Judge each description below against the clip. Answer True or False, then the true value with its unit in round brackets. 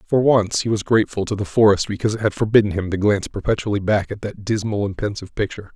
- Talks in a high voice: False (105 Hz)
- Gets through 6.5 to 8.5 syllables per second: True (7.0 syllables/s)